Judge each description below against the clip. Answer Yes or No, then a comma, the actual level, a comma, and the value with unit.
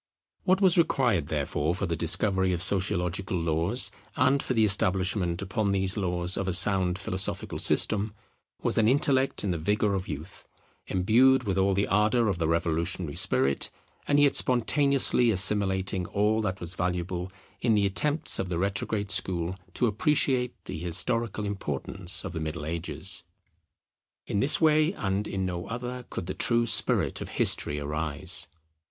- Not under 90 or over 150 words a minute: No, average, 160 wpm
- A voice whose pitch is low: Yes, very low, 95 Hz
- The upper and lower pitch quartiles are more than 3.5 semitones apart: Yes, average, 4.2 semitones